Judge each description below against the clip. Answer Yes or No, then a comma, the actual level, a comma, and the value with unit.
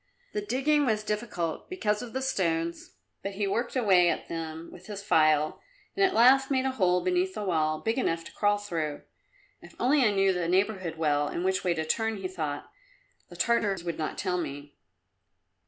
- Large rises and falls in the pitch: Yes, wide, 6.1 semitones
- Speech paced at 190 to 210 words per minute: Yes, average, 195 wpm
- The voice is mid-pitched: No, high, 195 Hz